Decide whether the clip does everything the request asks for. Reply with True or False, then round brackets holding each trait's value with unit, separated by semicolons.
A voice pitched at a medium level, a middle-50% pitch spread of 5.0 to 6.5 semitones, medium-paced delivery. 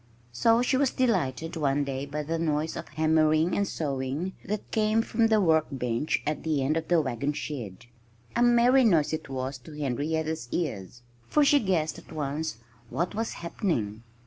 True (155 Hz; 5.5 semitones; 170 wpm)